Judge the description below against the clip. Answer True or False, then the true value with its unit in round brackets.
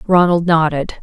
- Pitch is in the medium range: True (165 Hz)